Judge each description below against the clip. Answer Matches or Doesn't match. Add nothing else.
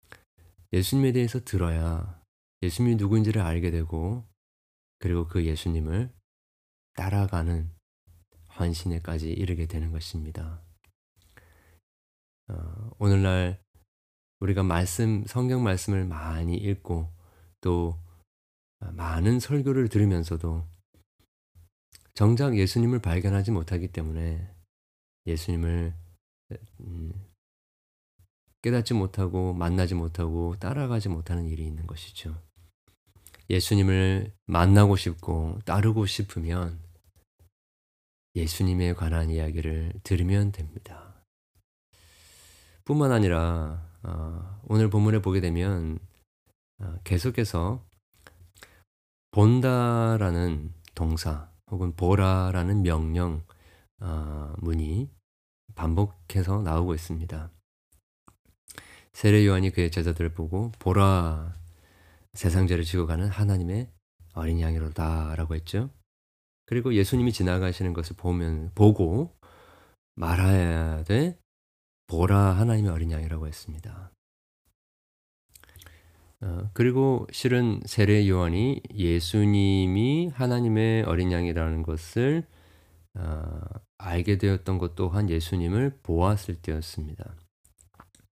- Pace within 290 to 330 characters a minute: Doesn't match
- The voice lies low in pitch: Matches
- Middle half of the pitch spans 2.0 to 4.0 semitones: Matches